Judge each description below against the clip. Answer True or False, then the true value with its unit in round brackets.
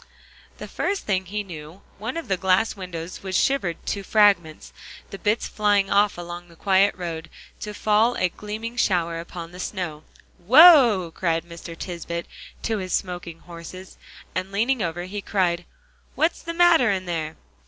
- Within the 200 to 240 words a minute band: False (165 wpm)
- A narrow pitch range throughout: False (3.5 semitones)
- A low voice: False (185 Hz)